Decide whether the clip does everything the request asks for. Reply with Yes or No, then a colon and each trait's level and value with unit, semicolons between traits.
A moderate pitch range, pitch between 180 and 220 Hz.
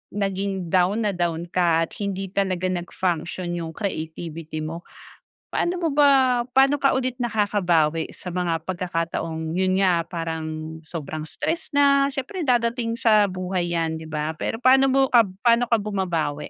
No: wide, 6.0 semitones; medium, 185 Hz